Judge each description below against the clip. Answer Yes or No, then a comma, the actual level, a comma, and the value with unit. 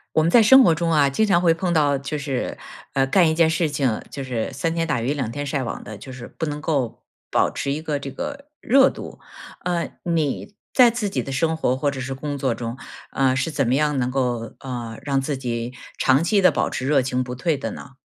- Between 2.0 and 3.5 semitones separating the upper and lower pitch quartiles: No, average, 3.9 semitones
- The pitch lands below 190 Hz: Yes, medium, 140 Hz